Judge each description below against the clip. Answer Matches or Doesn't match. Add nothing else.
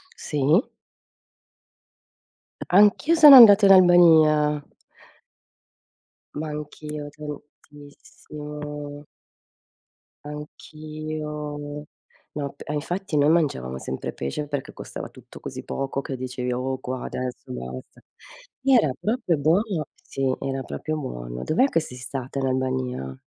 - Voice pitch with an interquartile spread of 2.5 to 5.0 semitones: Matches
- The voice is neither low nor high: Matches